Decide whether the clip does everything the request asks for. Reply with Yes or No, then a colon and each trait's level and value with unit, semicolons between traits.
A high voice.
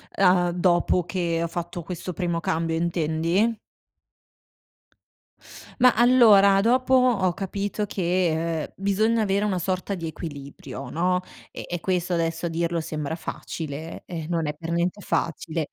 No: medium, 175 Hz